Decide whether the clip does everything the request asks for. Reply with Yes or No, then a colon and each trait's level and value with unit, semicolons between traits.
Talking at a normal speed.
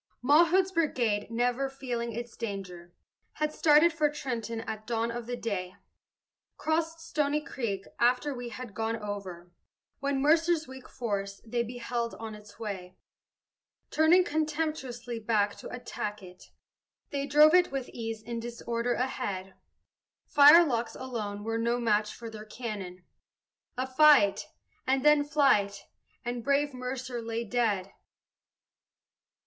No: slow, 130 wpm